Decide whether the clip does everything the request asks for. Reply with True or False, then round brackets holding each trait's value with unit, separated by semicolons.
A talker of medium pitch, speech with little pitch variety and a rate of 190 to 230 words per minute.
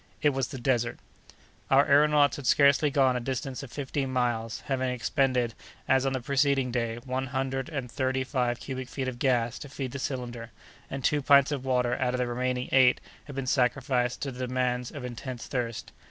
False (130 Hz; 1.6 semitones; 195 wpm)